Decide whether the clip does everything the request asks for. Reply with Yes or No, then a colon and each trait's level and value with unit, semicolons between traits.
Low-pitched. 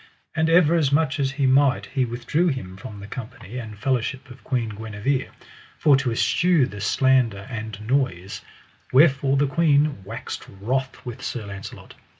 Yes: low, 130 Hz